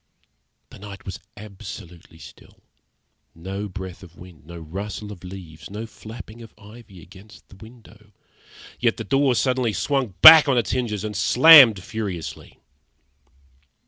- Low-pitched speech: Yes, low, 105 Hz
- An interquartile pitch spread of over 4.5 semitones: No, average, 3.7 semitones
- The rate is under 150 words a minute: Yes, average, 140 wpm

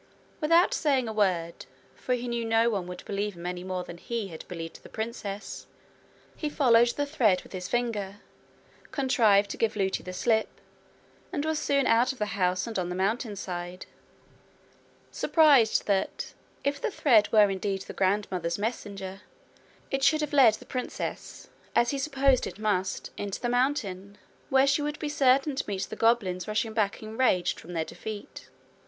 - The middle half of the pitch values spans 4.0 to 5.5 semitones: Yes, average, 5.2 semitones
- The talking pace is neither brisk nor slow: Yes, average, 170 wpm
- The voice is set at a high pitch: Yes, high, 220 Hz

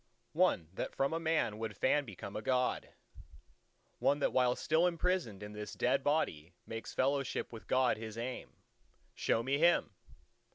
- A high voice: No, low, 125 Hz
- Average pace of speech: Yes, average, 160 wpm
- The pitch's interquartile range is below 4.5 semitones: No, average, 5.1 semitones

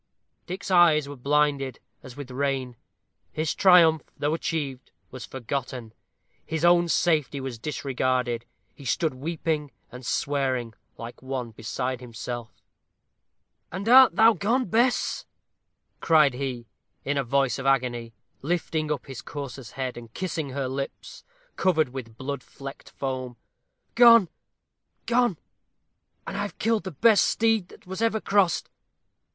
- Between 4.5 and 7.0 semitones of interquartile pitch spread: Yes, average, 5.2 semitones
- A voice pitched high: No, medium, 140 Hz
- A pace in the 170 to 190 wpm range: No, slow, 135 wpm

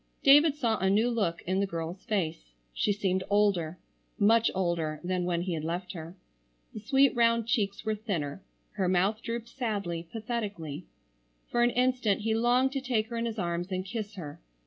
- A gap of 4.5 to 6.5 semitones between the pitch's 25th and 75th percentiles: Yes, average, 4.8 semitones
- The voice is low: No, high, 205 Hz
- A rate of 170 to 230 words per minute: Yes, average, 185 wpm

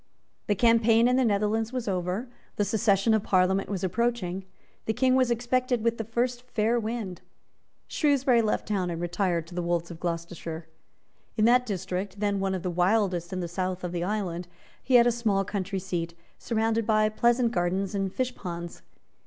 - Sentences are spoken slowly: No, average, 185 wpm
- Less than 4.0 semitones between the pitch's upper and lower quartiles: No, average, 4.3 semitones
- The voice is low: No, high, 205 Hz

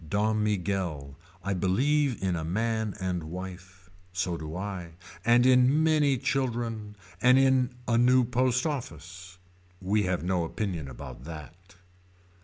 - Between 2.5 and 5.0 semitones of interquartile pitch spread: No, wide, 5.6 semitones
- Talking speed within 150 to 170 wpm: No, slow, 135 wpm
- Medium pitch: No, low, 100 Hz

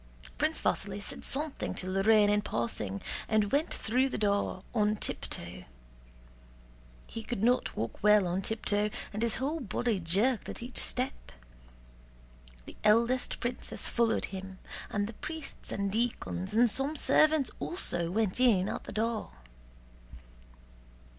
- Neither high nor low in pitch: No, high, 215 Hz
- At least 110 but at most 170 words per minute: Yes, average, 140 wpm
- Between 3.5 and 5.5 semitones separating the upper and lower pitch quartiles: Yes, average, 3.8 semitones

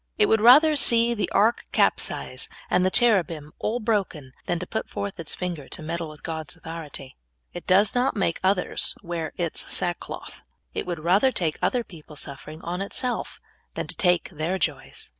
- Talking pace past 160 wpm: Yes, average, 180 wpm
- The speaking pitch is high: No, medium, 180 Hz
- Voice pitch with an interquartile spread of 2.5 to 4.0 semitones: No, average, 5.1 semitones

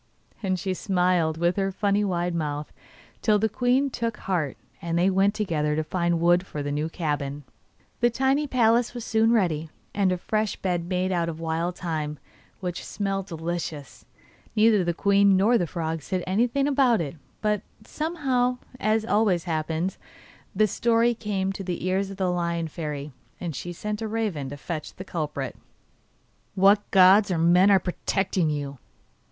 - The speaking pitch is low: No, medium, 185 Hz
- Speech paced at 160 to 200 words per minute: Yes, average, 170 wpm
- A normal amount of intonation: Yes, average, 4.3 semitones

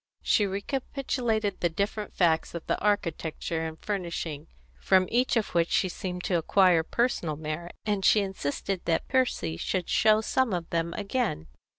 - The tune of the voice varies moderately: Yes, average, 4.1 semitones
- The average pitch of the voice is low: No, medium, 185 Hz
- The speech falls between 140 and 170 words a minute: Yes, average, 160 wpm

